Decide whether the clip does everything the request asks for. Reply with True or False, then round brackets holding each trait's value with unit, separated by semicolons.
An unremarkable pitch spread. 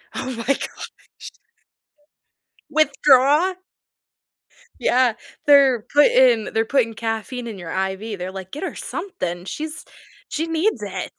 False (5.8 semitones)